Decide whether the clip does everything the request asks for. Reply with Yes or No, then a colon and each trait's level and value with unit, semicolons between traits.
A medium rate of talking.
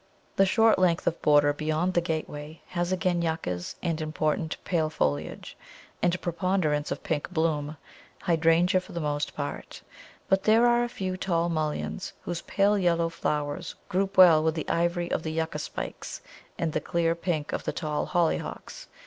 Yes: average, 170 wpm